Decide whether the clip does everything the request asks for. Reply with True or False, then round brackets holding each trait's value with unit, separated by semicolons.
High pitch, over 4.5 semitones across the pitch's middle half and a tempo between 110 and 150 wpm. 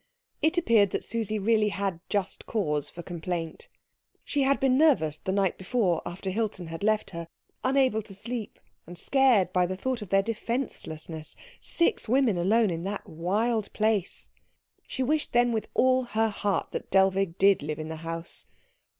False (200 Hz; 4.9 semitones; 170 wpm)